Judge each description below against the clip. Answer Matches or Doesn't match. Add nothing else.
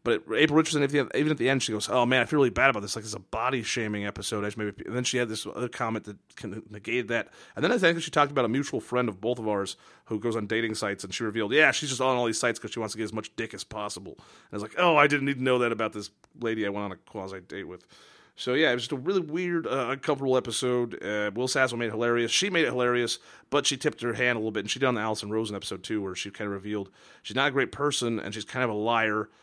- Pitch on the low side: Matches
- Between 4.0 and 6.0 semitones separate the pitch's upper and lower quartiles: Doesn't match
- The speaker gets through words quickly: Matches